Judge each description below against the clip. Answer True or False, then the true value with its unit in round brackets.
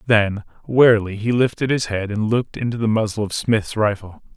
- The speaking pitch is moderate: False (110 Hz)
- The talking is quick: False (195 wpm)